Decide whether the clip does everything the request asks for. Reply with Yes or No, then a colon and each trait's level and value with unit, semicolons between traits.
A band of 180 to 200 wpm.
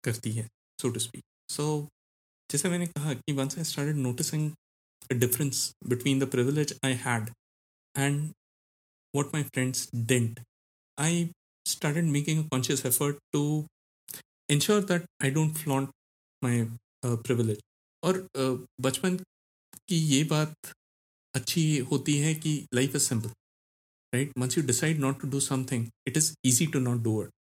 No: average, 145 wpm